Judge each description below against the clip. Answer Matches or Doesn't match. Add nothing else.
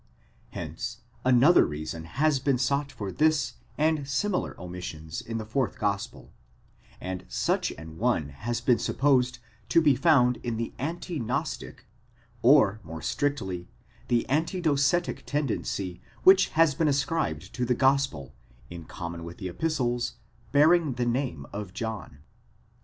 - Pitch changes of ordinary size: Doesn't match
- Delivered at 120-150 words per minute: Matches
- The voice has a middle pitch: Doesn't match